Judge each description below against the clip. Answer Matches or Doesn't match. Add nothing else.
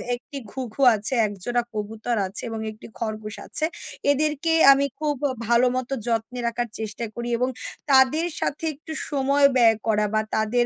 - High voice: Matches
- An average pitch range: Matches